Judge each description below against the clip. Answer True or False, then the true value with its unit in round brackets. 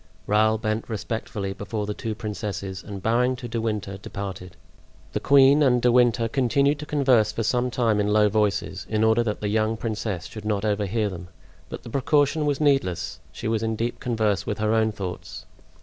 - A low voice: True (110 Hz)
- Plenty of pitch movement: False (2.8 semitones)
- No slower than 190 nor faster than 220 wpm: True (195 wpm)